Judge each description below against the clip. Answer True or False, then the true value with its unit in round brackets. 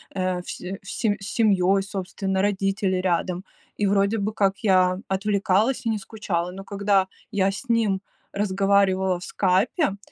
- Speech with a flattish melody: True (1.4 semitones)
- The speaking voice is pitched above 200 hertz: False (195 Hz)